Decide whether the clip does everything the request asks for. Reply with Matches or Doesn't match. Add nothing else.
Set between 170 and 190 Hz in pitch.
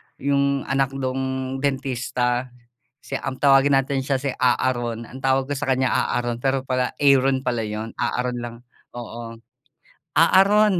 Doesn't match